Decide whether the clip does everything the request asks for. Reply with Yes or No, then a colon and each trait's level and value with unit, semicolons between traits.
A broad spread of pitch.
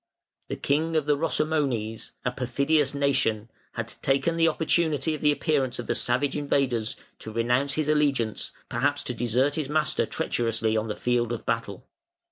No: average, 4.0 semitones